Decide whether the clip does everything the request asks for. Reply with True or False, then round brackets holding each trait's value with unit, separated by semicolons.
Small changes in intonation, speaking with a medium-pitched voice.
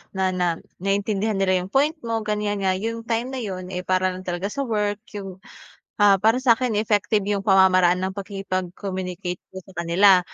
False (2.3 semitones; 195 Hz)